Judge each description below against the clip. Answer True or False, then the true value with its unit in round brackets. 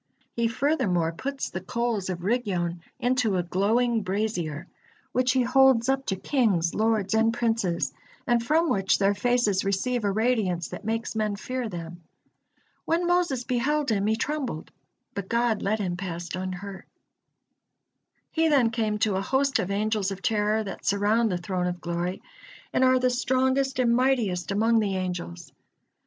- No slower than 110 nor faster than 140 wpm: False (160 wpm)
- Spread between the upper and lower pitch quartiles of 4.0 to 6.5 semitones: True (4.7 semitones)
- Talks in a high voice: True (220 Hz)